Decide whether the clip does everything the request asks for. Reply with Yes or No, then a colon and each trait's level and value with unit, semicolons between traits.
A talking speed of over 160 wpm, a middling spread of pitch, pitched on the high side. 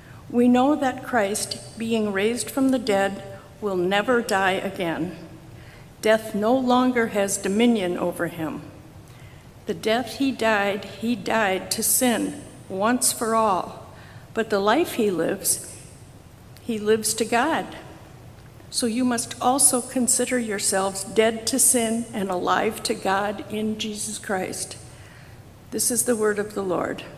No: average, 140 wpm; average, 3.6 semitones; high, 220 Hz